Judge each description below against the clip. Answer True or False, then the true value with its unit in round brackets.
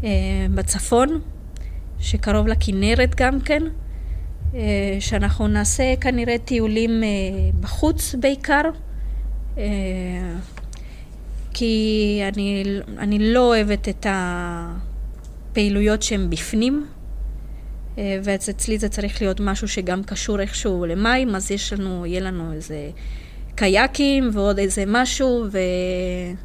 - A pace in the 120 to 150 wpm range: False (100 wpm)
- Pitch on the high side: True (195 Hz)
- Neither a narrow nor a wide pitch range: False (7.1 semitones)